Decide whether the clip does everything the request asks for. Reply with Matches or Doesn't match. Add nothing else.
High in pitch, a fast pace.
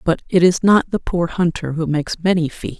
Doesn't match